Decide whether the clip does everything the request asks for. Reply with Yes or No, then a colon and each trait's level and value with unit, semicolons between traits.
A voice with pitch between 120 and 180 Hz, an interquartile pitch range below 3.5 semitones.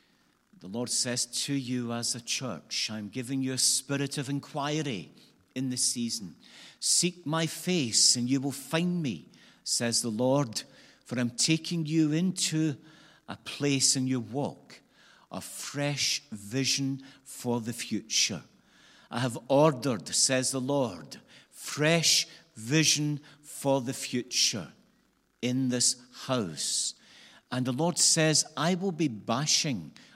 No: low, 135 Hz; average, 3.8 semitones